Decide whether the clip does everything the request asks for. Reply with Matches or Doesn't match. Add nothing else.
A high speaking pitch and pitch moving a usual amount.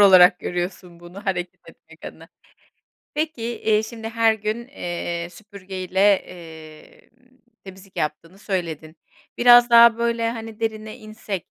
Matches